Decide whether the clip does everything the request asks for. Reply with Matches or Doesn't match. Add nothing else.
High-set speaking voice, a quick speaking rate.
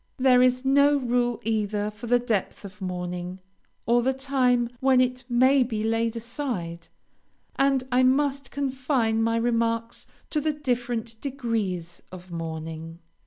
Doesn't match